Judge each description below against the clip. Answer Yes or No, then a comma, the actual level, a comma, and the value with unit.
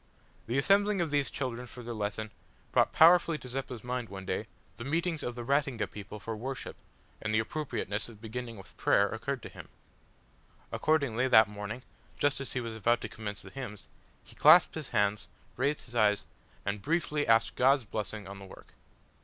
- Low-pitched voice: Yes, low, 120 Hz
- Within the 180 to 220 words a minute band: Yes, average, 185 wpm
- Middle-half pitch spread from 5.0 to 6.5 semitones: No, average, 4.5 semitones